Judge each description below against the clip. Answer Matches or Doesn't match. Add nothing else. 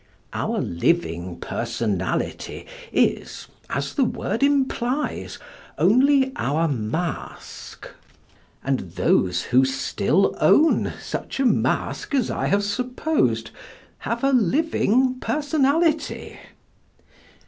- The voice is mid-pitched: Doesn't match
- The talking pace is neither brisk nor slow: Doesn't match